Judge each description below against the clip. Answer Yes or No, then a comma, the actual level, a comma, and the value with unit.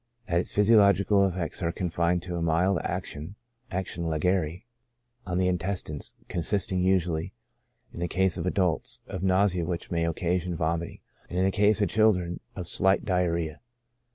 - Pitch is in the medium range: No, very low, 90 Hz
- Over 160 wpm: No, average, 155 wpm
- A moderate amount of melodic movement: No, narrow, 2.2 semitones